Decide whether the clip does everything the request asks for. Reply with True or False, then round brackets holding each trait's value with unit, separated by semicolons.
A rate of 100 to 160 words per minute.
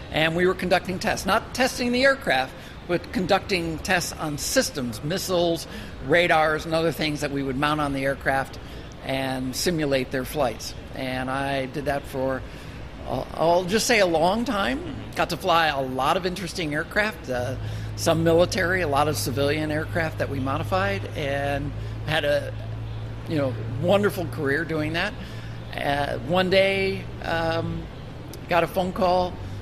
True (155 wpm)